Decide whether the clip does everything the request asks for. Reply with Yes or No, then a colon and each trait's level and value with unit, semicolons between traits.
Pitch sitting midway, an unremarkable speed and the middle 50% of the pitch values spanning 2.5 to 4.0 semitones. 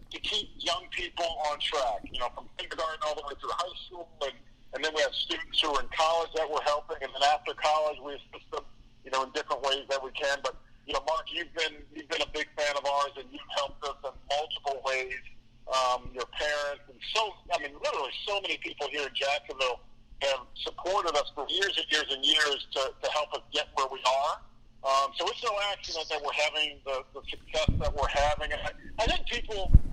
No: medium, 145 Hz; fast, 225 wpm; average, 2.9 semitones